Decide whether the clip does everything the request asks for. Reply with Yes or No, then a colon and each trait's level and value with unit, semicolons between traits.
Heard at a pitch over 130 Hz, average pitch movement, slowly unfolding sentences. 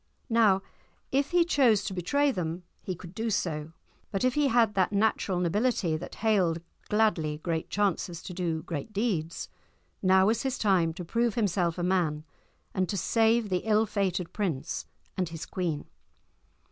No: high, 190 Hz; average, 4.5 semitones; average, 165 wpm